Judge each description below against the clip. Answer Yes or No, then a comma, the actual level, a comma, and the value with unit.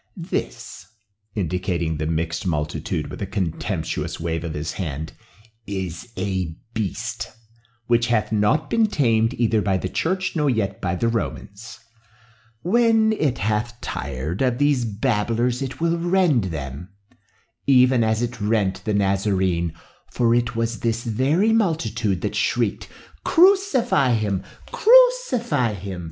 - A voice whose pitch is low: Yes, low, 110 Hz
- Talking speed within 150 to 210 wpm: No, slow, 135 wpm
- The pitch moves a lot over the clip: Yes, wide, 5.9 semitones